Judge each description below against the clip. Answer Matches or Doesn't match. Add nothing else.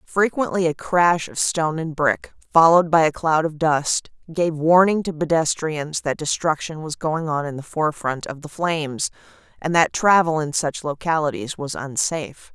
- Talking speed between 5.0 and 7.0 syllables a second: Doesn't match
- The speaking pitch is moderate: Matches